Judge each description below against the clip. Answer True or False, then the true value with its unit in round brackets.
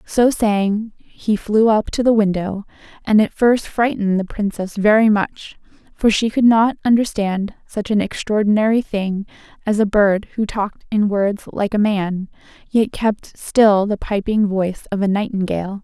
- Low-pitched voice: False (210 Hz)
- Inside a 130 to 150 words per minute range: False (165 wpm)